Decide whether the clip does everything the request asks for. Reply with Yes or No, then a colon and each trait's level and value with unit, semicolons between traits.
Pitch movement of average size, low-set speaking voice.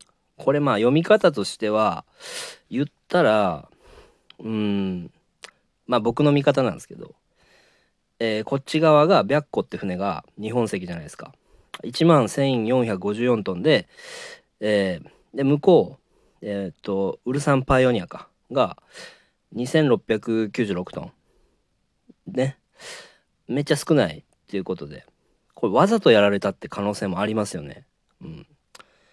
Yes: average, 5.0 semitones; low, 120 Hz